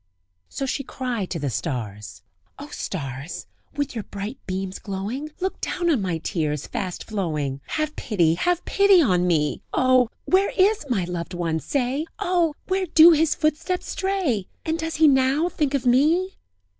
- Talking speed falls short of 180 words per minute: Yes, average, 165 wpm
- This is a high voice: Yes, very high, 255 Hz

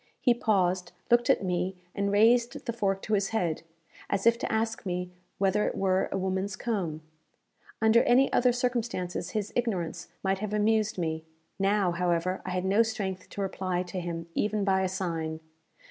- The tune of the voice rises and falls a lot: No, average, 3.4 semitones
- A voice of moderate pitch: No, high, 195 Hz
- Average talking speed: Yes, average, 175 wpm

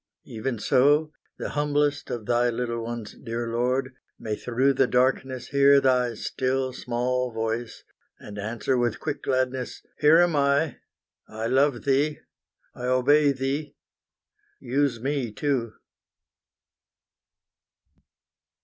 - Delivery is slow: Yes, slow, 115 wpm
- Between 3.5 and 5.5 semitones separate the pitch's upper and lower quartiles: No, average, 2.9 semitones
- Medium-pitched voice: No, low, 130 Hz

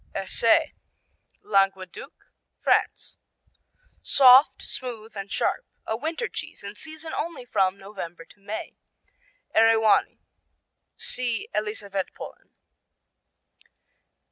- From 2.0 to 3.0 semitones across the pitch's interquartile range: No, average, 4.3 semitones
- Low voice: No, high, 215 Hz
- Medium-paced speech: No, slow, 85 wpm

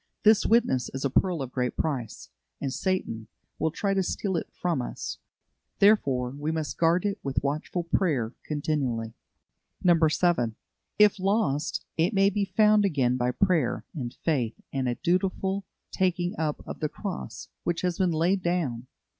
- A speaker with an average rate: Yes, average, 160 wpm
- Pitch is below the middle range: No, medium, 165 Hz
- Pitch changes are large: Yes, wide, 6.1 semitones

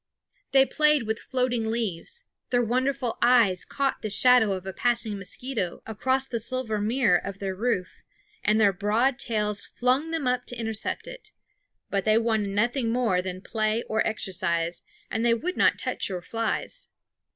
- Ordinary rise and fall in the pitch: Yes, average, 3.7 semitones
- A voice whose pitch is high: Yes, high, 225 Hz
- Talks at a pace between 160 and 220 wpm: Yes, average, 165 wpm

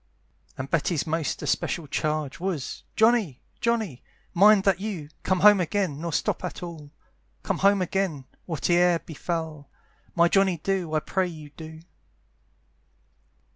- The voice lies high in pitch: No, medium, 170 Hz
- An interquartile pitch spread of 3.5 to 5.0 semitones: Yes, average, 3.8 semitones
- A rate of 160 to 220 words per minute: No, slow, 135 wpm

